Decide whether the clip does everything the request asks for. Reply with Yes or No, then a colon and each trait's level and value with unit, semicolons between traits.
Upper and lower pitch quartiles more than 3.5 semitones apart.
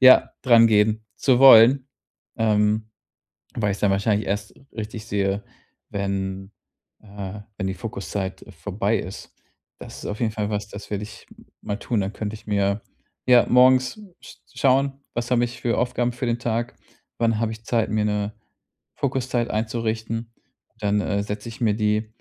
No: narrow, 2.5 semitones